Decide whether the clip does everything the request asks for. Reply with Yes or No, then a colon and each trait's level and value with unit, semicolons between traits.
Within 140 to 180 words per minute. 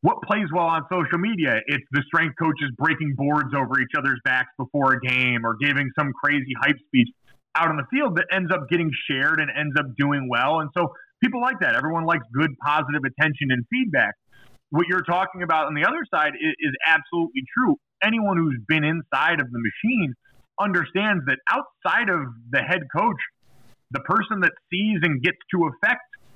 No: average, 195 wpm